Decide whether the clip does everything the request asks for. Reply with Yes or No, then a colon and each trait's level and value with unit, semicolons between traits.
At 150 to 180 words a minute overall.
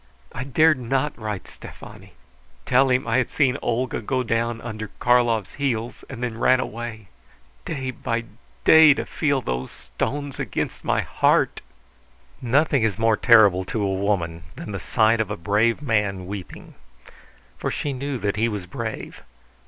Yes: average, 160 wpm